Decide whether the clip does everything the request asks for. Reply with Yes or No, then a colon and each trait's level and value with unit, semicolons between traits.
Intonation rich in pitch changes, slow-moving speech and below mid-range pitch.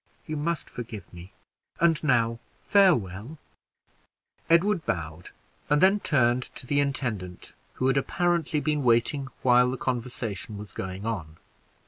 Yes: wide, 6.2 semitones; slow, 130 wpm; low, 125 Hz